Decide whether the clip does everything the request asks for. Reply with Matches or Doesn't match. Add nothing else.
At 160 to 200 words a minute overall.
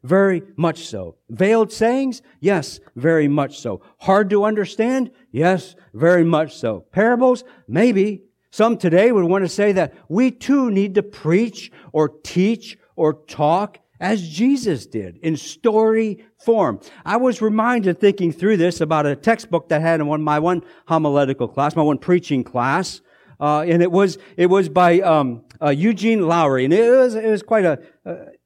Matches